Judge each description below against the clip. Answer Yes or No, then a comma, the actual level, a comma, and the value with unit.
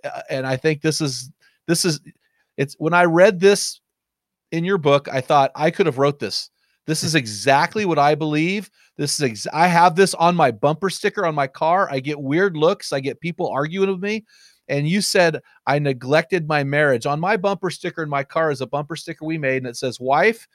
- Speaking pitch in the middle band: Yes, medium, 155 Hz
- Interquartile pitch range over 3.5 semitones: Yes, average, 3.9 semitones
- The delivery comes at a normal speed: No, fast, 220 wpm